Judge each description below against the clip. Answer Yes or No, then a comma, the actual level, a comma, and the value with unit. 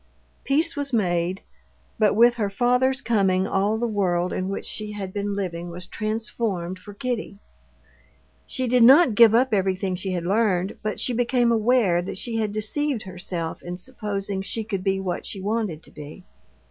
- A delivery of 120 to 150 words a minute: No, average, 175 wpm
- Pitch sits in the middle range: No, high, 205 Hz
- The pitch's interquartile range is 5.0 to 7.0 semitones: No, average, 3.9 semitones